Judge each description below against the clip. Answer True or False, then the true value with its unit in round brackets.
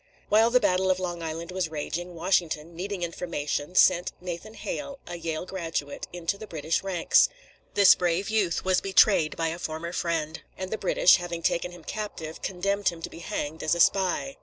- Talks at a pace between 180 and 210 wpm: True (185 wpm)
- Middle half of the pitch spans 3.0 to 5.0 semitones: False (2.4 semitones)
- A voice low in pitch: False (175 Hz)